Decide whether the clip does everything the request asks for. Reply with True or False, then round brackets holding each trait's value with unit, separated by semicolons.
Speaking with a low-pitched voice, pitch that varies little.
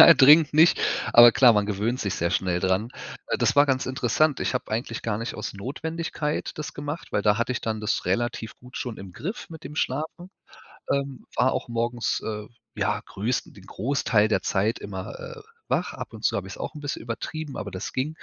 False (120 Hz; 5.5 semitones)